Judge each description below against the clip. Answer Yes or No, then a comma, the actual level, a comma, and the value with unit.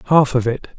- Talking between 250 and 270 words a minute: No, fast, 230 wpm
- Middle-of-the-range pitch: No, low, 130 Hz